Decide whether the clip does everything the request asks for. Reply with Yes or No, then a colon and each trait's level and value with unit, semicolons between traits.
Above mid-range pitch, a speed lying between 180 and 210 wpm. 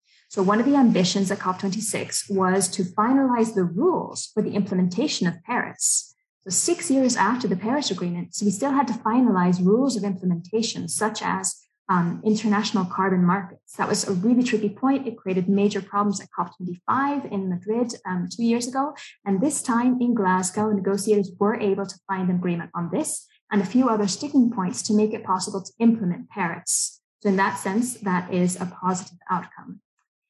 Yes: high, 205 Hz; average, 185 wpm